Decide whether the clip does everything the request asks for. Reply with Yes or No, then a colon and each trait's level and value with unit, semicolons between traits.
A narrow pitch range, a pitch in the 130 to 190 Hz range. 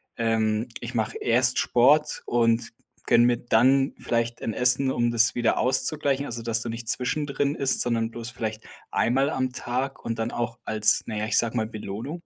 No: narrow, 2.3 semitones; low, 120 Hz